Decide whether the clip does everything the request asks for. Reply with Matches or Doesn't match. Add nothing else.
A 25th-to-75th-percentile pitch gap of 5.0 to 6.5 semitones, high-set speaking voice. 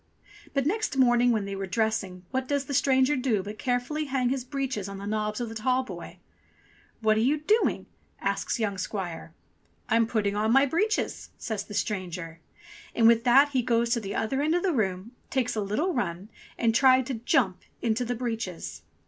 Doesn't match